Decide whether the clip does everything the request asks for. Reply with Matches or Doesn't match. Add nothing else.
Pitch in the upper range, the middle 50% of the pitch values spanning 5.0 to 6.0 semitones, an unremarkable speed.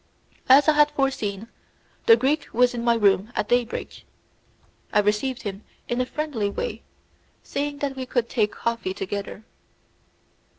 Doesn't match